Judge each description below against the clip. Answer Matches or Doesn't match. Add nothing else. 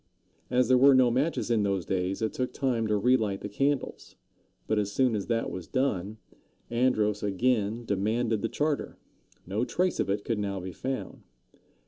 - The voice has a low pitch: Matches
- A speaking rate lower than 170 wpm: Doesn't match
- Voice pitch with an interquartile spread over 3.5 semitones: Matches